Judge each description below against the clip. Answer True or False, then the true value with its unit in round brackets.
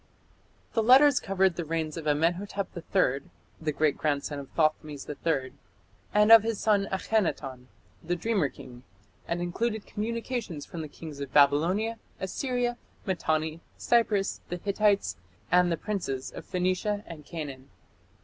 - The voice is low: False (175 Hz)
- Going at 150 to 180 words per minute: False (140 wpm)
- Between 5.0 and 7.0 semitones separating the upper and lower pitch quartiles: True (5.6 semitones)